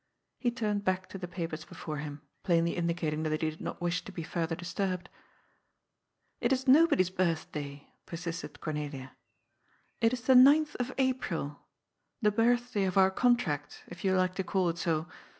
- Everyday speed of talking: Yes, average, 170 wpm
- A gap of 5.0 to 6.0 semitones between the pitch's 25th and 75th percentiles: Yes, average, 5.3 semitones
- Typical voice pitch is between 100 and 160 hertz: No, medium, 180 Hz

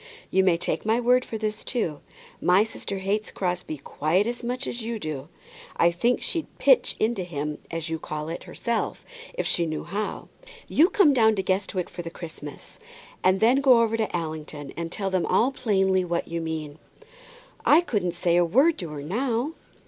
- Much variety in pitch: Yes, wide, 5.7 semitones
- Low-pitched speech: No, high, 190 Hz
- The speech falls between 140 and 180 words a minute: No, average, 190 wpm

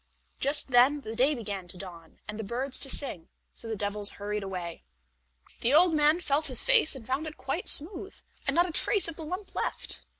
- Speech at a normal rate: No, fast, 210 wpm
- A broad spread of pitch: Yes, wide, 7.0 semitones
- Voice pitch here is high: Yes, very high, 265 Hz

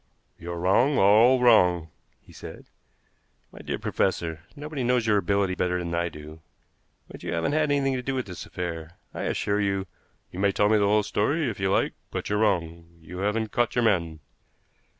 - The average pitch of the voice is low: Yes, low, 100 Hz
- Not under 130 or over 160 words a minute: No, average, 195 wpm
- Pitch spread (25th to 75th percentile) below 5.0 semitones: No, wide, 5.5 semitones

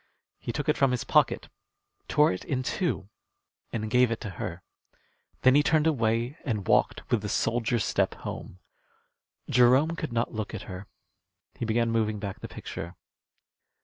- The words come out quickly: No, average, 165 wpm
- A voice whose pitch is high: No, low, 115 Hz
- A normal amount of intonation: Yes, average, 3.4 semitones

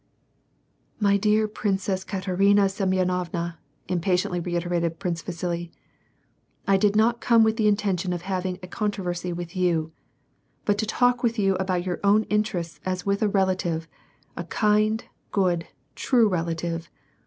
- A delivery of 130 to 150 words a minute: Yes, average, 145 wpm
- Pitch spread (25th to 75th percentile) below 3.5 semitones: Yes, average, 3.0 semitones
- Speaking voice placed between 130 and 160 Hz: No, medium, 185 Hz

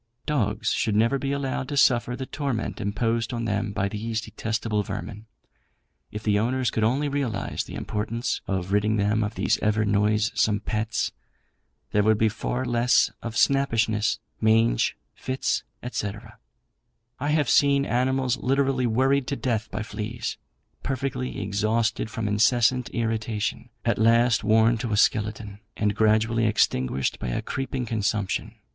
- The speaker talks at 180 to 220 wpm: No, average, 145 wpm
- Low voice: Yes, low, 110 Hz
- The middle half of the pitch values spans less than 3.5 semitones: Yes, average, 2.9 semitones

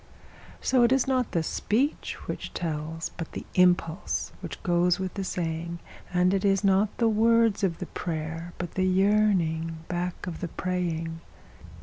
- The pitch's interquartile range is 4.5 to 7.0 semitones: No, average, 3.4 semitones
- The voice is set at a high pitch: No, medium, 180 Hz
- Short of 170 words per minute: Yes, average, 160 wpm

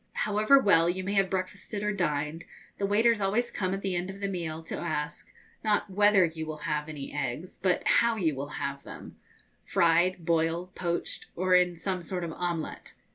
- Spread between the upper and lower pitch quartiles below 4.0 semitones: Yes, average, 3.4 semitones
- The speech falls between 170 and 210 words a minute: Yes, average, 190 wpm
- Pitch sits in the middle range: Yes, medium, 180 Hz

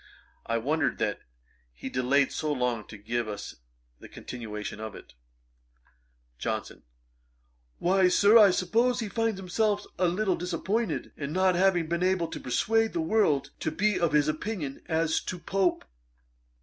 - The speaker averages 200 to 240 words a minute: No, average, 150 wpm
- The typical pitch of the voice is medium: Yes, medium, 175 Hz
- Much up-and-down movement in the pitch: Yes, wide, 6.5 semitones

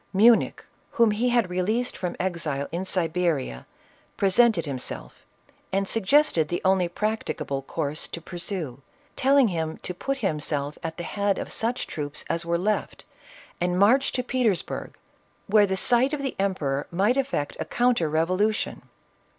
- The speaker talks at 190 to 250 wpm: No, average, 150 wpm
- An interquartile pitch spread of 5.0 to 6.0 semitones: Yes, wide, 5.6 semitones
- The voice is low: No, medium, 185 Hz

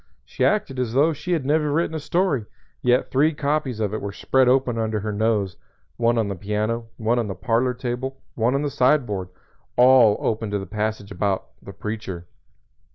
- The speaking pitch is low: Yes, low, 120 Hz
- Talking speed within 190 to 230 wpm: Yes, average, 195 wpm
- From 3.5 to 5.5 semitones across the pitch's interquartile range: Yes, average, 4.0 semitones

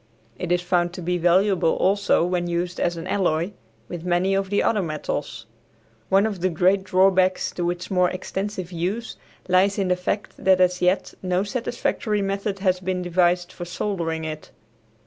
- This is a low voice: No, medium, 180 Hz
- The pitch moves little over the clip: Yes, narrow, 1.8 semitones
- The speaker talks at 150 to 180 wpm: Yes, average, 175 wpm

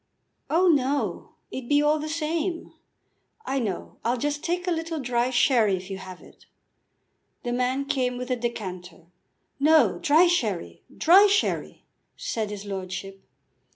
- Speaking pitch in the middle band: No, very high, 255 Hz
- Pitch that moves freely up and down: Yes, wide, 7.3 semitones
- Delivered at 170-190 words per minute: No, average, 150 wpm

